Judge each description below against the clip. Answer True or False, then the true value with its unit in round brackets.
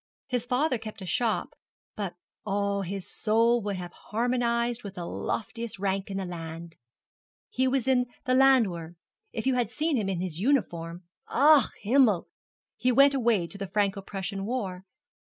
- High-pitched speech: True (215 Hz)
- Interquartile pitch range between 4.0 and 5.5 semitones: True (4.6 semitones)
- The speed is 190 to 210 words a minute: False (165 wpm)